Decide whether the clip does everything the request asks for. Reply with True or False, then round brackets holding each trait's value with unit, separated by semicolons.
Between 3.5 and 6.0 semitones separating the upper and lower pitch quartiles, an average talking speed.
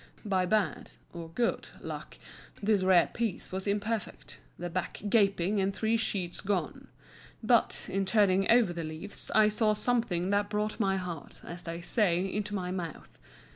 False (3.0 semitones; 155 wpm)